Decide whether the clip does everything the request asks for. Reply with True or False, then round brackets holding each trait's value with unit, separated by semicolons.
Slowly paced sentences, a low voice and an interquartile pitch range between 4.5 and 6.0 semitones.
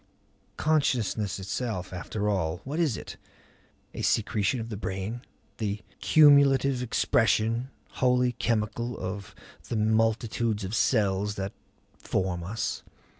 False (115 wpm; 110 Hz; 3.7 semitones)